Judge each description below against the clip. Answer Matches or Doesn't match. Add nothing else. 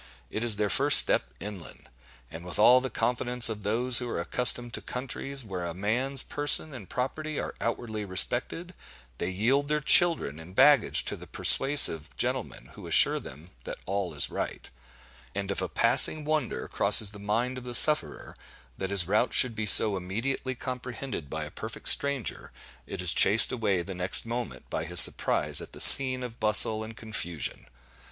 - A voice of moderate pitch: Doesn't match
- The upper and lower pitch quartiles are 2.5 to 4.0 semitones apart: Doesn't match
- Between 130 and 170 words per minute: Doesn't match